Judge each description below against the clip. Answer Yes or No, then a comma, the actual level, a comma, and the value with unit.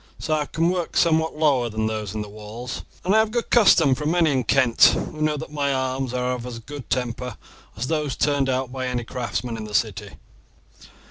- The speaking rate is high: Yes, fast, 215 wpm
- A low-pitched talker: Yes, low, 130 Hz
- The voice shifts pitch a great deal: No, average, 4.2 semitones